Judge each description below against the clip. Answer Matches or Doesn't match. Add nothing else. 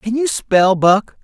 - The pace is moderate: Matches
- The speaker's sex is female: Doesn't match